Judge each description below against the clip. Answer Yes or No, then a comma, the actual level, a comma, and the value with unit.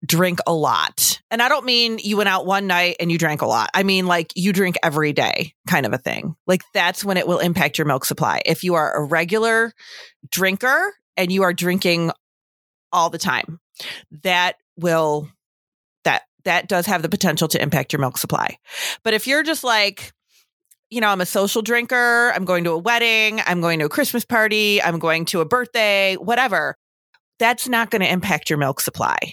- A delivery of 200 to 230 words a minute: Yes, fast, 205 wpm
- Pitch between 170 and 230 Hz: Yes, medium, 185 Hz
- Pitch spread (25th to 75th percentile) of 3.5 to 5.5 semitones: Yes, average, 5.2 semitones